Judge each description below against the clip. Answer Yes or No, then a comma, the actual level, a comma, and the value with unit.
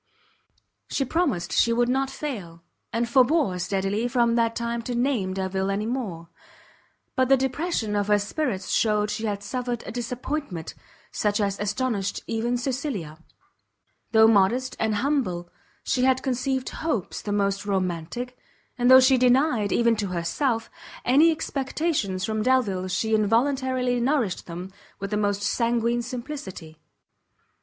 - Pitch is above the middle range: Yes, high, 230 Hz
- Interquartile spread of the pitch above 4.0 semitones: Yes, average, 4.4 semitones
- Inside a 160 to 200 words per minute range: No, average, 140 wpm